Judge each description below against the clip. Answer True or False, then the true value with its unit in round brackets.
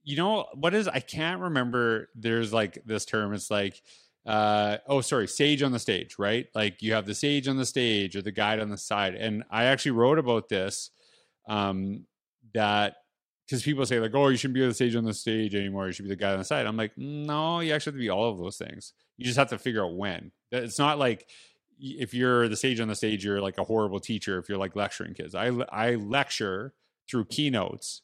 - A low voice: True (115 Hz)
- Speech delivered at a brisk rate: True (235 wpm)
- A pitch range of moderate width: True (4.1 semitones)